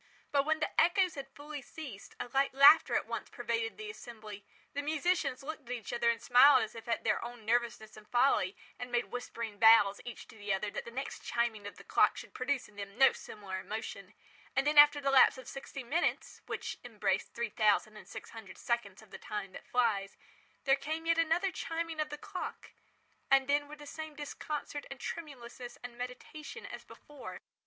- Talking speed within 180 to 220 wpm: Yes, fast, 205 wpm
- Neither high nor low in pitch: No, very high, 255 Hz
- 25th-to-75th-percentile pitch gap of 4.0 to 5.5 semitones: Yes, average, 4.9 semitones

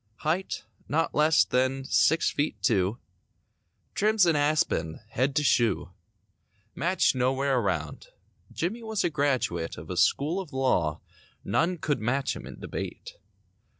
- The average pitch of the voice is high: No, medium, 140 Hz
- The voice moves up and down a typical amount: No, wide, 6.1 semitones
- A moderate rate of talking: No, slow, 130 wpm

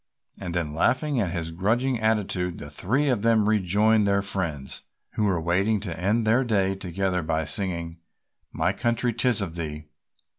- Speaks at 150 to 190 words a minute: Yes, average, 170 wpm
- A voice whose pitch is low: Yes, very low, 95 Hz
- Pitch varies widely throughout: No, average, 4.5 semitones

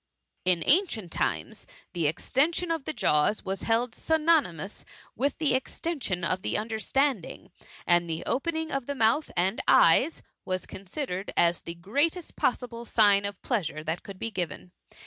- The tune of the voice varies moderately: No, wide, 8.0 semitones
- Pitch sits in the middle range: No, high, 220 Hz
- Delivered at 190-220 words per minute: No, average, 155 wpm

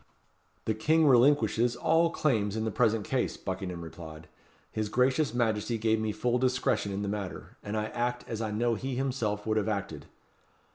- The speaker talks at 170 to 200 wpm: Yes, average, 180 wpm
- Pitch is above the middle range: No, low, 110 Hz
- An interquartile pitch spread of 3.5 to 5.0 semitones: No, average, 3.1 semitones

